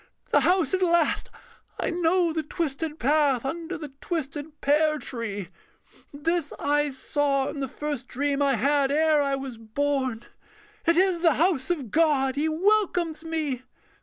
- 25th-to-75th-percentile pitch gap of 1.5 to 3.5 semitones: Yes, average, 3.2 semitones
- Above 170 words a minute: No, average, 155 wpm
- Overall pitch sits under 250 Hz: No, very high, 295 Hz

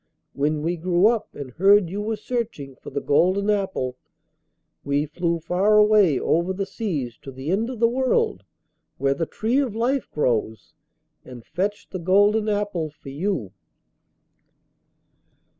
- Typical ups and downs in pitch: No, wide, 6.3 semitones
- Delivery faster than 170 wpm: No, average, 150 wpm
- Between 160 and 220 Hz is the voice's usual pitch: Yes, medium, 185 Hz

